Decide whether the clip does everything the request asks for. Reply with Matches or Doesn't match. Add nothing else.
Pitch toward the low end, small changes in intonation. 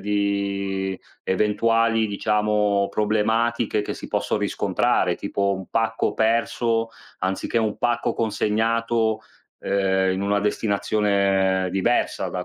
Matches